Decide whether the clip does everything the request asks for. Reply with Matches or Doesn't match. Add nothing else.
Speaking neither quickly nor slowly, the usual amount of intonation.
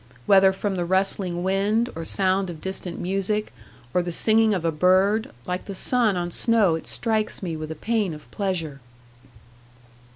Matches